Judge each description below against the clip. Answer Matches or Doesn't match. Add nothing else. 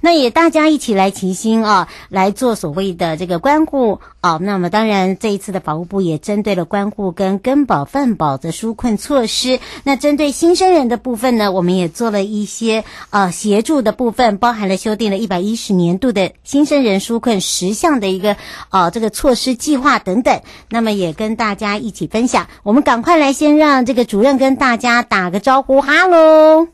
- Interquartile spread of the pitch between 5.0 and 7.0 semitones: Matches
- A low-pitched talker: Doesn't match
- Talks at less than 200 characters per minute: Doesn't match